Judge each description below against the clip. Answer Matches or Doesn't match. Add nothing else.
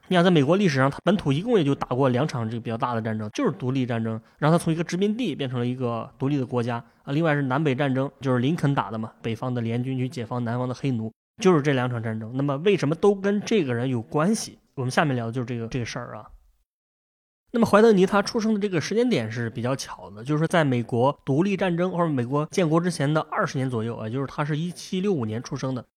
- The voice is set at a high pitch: Doesn't match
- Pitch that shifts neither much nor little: Doesn't match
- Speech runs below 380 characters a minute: Doesn't match